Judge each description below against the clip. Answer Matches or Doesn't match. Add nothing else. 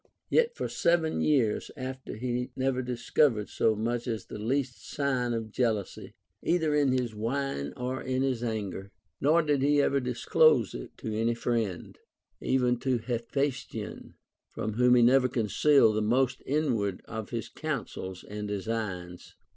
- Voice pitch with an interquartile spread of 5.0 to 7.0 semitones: Doesn't match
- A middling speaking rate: Matches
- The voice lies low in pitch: Matches